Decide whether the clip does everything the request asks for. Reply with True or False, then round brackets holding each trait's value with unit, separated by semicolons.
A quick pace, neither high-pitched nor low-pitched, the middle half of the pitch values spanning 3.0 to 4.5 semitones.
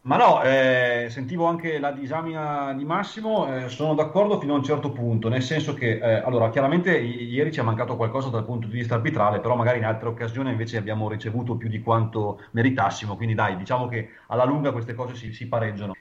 False (210 wpm; 120 Hz; 3.8 semitones)